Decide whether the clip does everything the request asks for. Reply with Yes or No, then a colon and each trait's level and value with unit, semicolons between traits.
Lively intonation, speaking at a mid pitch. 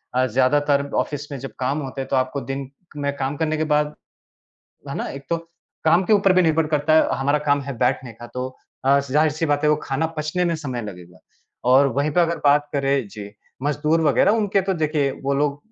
No: narrow, 2.5 semitones; medium, 145 Hz